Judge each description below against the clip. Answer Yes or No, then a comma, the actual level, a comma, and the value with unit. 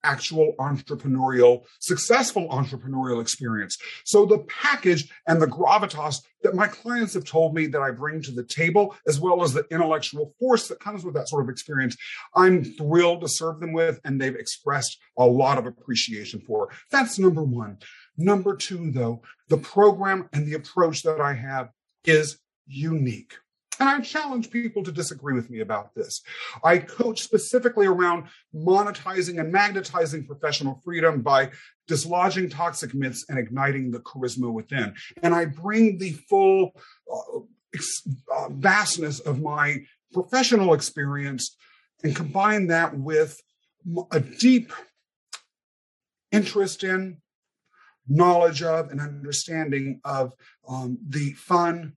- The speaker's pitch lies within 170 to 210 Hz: No, medium, 160 Hz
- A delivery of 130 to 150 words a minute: Yes, average, 145 wpm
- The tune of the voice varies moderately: No, wide, 5.7 semitones